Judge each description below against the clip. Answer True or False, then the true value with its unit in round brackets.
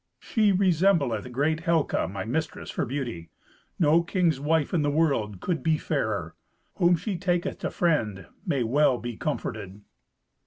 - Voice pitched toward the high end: False (150 Hz)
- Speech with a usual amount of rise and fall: False (6.4 semitones)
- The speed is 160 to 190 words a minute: False (150 wpm)